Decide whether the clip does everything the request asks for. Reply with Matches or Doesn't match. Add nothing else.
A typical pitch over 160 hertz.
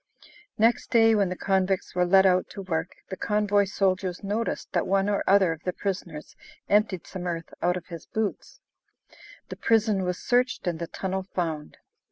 Matches